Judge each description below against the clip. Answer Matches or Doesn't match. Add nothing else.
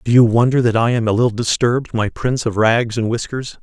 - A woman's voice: Doesn't match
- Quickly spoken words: Matches